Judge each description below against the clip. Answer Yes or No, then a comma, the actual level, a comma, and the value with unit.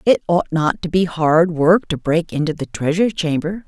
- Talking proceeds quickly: Yes, fast, 210 wpm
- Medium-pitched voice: Yes, medium, 165 Hz